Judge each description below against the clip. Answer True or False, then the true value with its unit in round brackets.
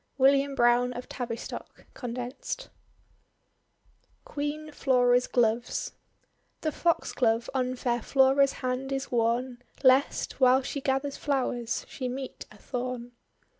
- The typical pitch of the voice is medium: False (255 Hz)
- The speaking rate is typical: False (110 wpm)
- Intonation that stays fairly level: True (1.9 semitones)